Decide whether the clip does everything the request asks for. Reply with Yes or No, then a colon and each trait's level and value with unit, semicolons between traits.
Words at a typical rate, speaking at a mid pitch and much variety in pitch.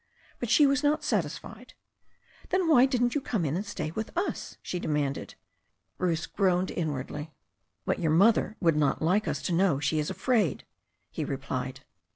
Yes: average, 175 wpm; medium, 180 Hz; wide, 7.5 semitones